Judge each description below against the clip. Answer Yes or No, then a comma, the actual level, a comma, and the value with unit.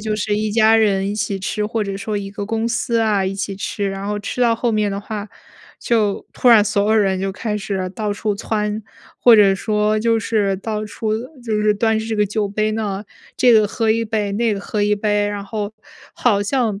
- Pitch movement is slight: Yes, narrow, 1.5 semitones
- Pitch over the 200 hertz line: Yes, high, 210 Hz